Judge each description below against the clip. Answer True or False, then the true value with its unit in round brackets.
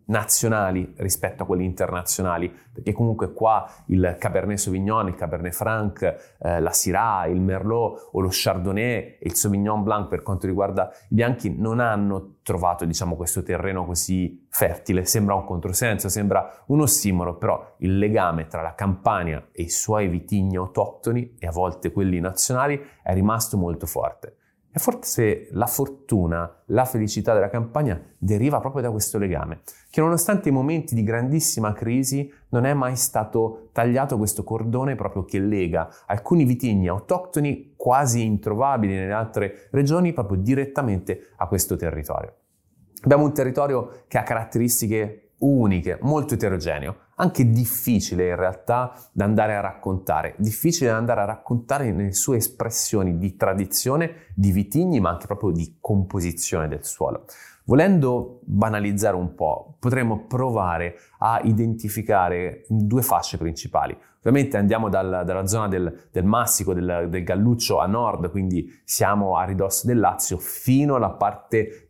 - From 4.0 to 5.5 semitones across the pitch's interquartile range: True (4.5 semitones)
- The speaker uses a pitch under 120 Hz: True (105 Hz)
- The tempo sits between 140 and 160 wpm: True (150 wpm)